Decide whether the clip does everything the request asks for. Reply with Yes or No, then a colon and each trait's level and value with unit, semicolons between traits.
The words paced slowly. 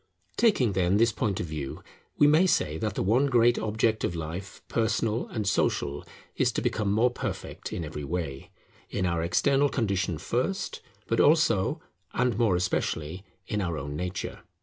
No: average, 170 wpm